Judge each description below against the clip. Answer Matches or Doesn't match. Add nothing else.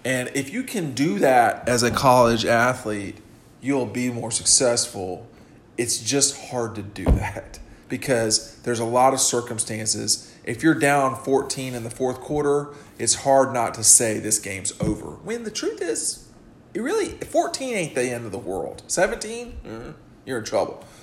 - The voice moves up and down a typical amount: Matches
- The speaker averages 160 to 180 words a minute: Matches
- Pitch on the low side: Matches